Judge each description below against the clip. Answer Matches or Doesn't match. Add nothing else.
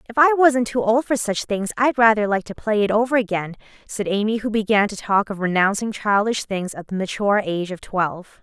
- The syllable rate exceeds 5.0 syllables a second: Matches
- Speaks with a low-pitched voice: Doesn't match